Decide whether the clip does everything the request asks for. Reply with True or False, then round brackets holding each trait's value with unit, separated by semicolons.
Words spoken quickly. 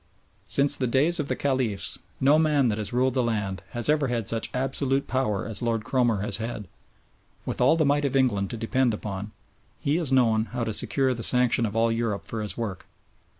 True (210 wpm)